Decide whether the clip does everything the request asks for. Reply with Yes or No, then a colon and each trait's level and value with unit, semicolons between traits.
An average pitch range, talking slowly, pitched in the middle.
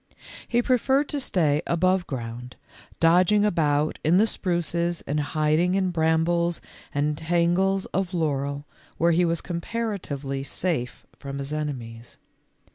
Yes: average, 4.0 semitones; slow, 130 wpm; medium, 165 Hz